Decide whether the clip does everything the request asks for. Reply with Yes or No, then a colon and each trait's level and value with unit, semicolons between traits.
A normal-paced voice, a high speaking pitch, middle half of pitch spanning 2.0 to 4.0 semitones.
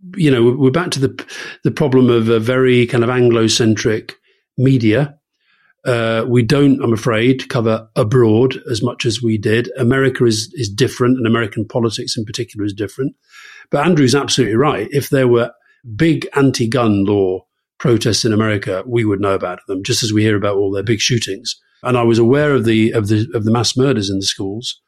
No: average, 195 wpm; low, 120 Hz; average, 2.9 semitones